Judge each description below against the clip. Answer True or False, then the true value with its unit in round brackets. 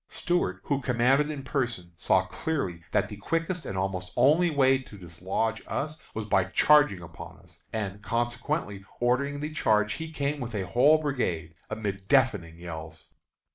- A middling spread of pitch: False (6.9 semitones)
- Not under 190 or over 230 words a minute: False (160 wpm)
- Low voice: True (120 Hz)